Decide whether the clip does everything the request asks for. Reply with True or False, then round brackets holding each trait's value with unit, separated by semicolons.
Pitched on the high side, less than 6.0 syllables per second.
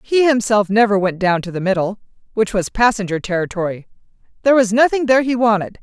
False (215 Hz; 6.3 syllables/s)